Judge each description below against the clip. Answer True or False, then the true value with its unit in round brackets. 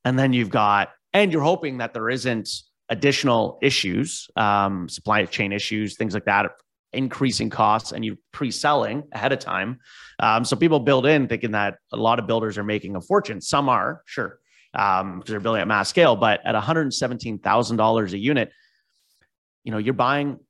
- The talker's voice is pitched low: True (115 Hz)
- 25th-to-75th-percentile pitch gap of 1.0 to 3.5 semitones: False (4.1 semitones)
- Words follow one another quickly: False (180 wpm)